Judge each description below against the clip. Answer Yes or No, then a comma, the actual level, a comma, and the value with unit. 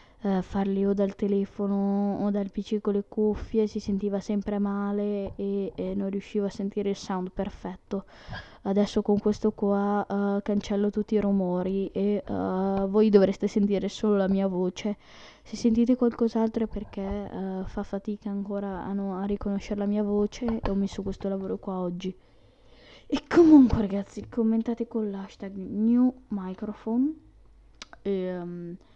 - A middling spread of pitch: No, narrow, 1.4 semitones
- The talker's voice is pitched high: Yes, high, 200 Hz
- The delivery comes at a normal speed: Yes, average, 155 wpm